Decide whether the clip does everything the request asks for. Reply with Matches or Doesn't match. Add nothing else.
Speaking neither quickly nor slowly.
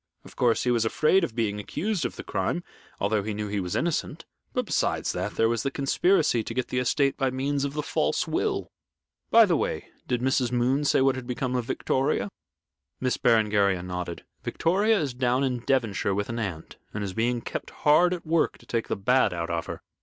Doesn't match